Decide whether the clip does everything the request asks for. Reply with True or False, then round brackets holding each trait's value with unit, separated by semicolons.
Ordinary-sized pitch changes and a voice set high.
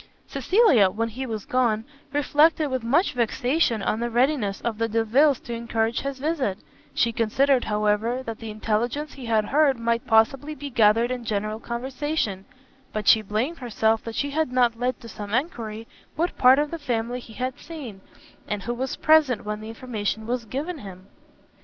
True (3.7 semitones; 235 Hz)